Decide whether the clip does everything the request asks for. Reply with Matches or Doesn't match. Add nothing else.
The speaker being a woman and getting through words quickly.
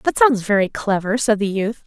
Matches